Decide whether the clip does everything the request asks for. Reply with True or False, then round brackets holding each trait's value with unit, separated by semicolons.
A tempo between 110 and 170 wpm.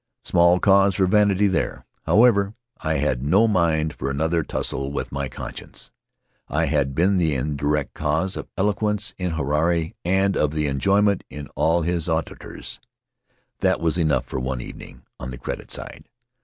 True (155 wpm)